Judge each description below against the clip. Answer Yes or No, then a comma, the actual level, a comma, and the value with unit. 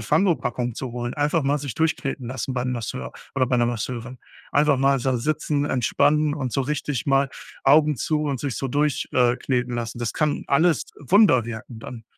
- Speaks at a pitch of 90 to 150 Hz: Yes, low, 135 Hz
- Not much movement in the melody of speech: No, average, 3.1 semitones